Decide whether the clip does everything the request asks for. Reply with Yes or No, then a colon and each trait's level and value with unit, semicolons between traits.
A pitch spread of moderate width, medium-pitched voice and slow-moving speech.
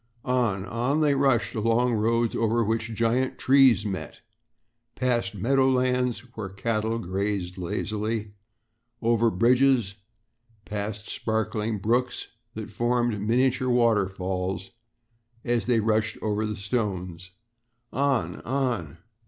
No: average, 3.2 semitones; low, 115 Hz; slow, 110 wpm